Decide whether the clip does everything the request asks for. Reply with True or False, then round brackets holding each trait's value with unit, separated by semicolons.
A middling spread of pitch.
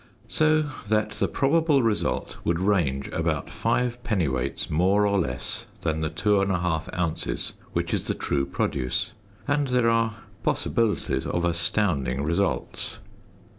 False (6.1 semitones)